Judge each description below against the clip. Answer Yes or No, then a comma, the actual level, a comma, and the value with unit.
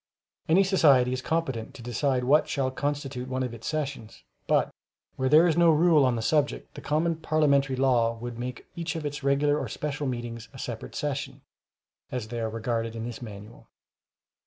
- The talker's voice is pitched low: Yes, low, 130 Hz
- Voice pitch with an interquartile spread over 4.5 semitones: No, average, 3.9 semitones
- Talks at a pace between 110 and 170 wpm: No, average, 185 wpm